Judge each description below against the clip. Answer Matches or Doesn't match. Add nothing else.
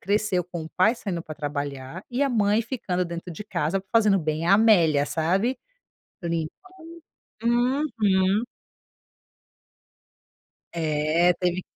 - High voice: Doesn't match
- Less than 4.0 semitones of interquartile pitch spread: Doesn't match